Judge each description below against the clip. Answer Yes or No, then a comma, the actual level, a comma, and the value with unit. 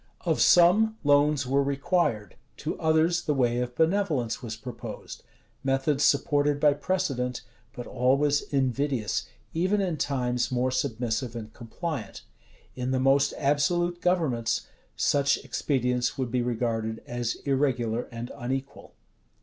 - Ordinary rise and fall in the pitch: Yes, average, 3.4 semitones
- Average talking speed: No, slow, 125 wpm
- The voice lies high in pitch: No, low, 135 Hz